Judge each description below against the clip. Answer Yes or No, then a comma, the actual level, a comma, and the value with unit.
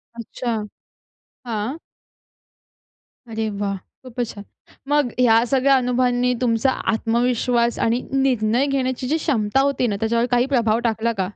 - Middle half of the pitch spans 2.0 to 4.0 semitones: Yes, narrow, 2.4 semitones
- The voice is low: No, high, 245 Hz